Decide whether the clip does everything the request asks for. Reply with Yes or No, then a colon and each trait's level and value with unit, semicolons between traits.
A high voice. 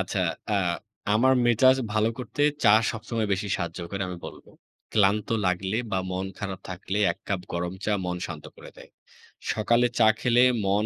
No: low, 100 Hz